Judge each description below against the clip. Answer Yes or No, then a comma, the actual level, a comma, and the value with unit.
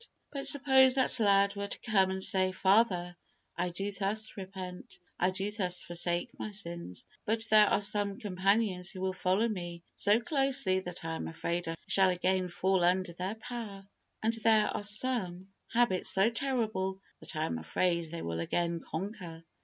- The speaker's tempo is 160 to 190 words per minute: Yes, average, 175 wpm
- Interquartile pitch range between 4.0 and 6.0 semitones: No, average, 3.3 semitones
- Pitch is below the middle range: No, high, 190 Hz